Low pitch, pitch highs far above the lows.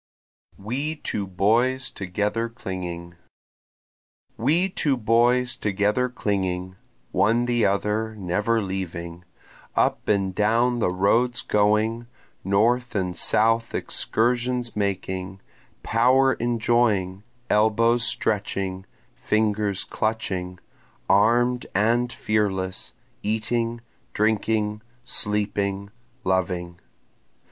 No: low, 105 Hz; average, 3.5 semitones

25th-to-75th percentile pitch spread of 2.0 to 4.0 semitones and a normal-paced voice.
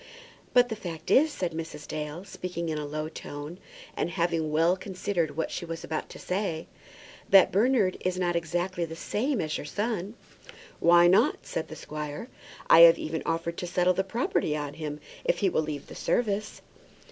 Yes: average, 3.3 semitones; average, 185 wpm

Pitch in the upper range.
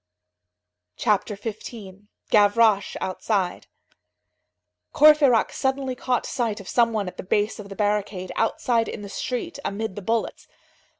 Yes: high, 215 Hz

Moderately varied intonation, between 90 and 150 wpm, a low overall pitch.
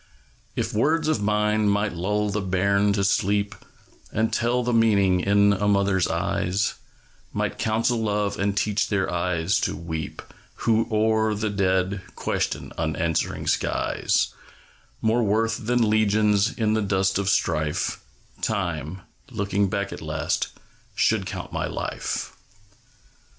No: narrow, 2.3 semitones; slow, 135 wpm; low, 100 Hz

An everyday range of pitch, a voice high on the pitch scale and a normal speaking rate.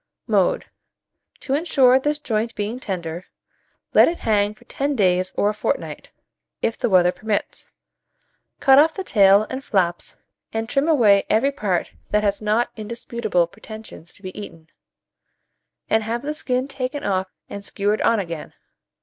Yes: average, 4.5 semitones; high, 215 Hz; average, 155 wpm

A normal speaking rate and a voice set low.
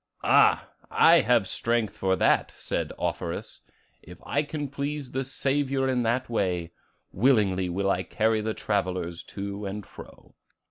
Yes: average, 145 wpm; low, 110 Hz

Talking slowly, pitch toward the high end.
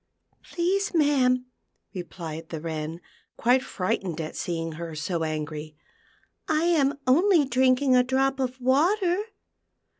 Yes: slow, 130 wpm; very high, 255 Hz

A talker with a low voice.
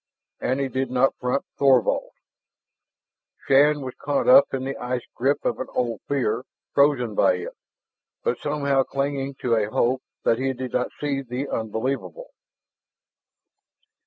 Yes: low, 130 Hz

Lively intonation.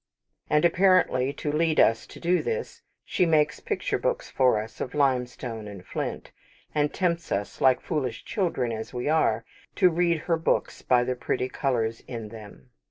Yes: wide, 6.1 semitones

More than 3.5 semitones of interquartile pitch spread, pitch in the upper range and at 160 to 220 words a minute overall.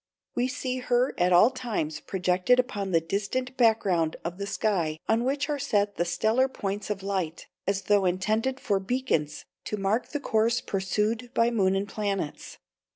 Yes: average, 4.4 semitones; high, 205 Hz; average, 170 wpm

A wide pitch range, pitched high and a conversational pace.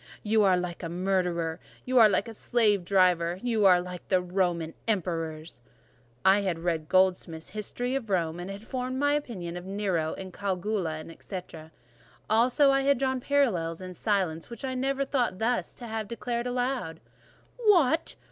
Yes: wide, 5.7 semitones; high, 195 Hz; average, 155 wpm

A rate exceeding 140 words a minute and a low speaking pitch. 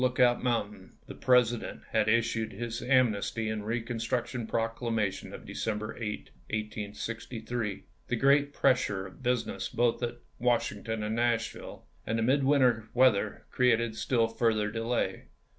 No: slow, 135 wpm; low, 115 Hz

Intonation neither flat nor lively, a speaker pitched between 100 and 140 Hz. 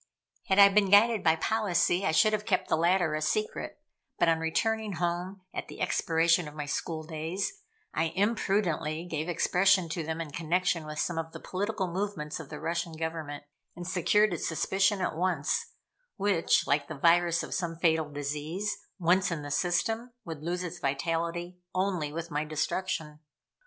No: average, 3.1 semitones; medium, 170 Hz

